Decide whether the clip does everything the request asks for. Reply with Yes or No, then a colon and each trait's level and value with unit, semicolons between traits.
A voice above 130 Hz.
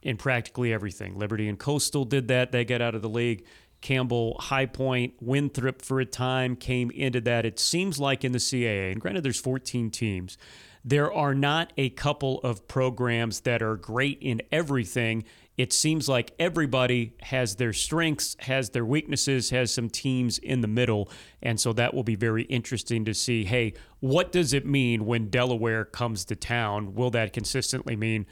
No: low, 125 Hz